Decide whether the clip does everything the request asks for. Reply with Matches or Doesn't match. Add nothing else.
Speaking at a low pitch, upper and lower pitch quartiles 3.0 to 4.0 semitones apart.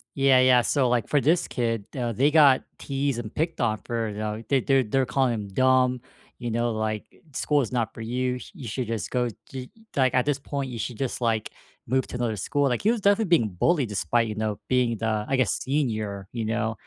Matches